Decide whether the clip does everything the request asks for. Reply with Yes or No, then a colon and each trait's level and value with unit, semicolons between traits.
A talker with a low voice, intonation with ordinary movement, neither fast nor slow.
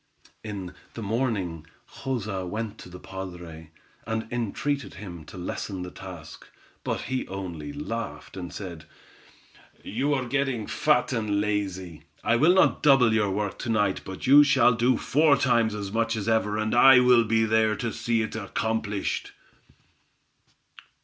Yes: low, 110 Hz; average, 4.0 semitones; average, 155 wpm